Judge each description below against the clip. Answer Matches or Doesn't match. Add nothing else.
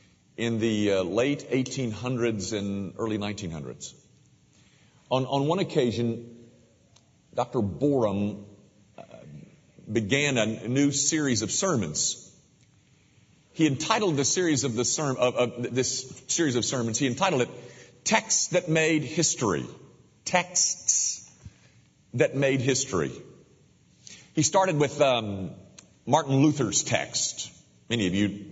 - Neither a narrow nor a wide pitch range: Matches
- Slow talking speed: Matches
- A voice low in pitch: Matches